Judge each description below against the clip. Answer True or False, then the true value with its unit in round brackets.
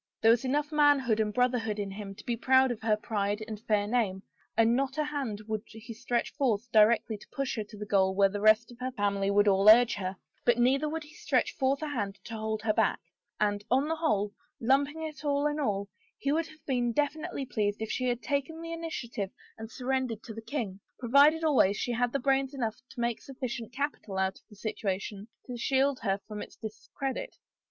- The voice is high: True (235 Hz)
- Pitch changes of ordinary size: True (4.5 semitones)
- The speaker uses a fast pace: True (225 wpm)